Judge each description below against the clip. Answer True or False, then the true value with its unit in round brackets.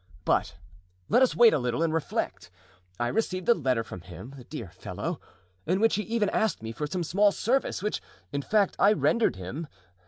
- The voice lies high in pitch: False (165 Hz)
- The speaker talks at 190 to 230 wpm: True (195 wpm)